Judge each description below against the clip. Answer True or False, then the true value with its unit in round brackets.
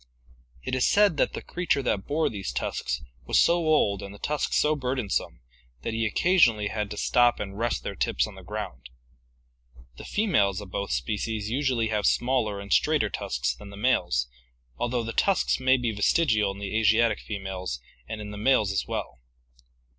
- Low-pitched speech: True (110 Hz)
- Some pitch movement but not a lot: True (4.5 semitones)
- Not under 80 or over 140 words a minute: False (185 wpm)